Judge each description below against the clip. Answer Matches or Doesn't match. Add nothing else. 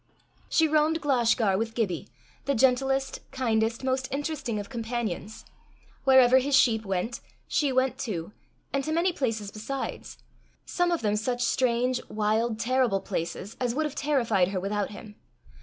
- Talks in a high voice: Matches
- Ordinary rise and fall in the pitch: Matches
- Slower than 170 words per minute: Matches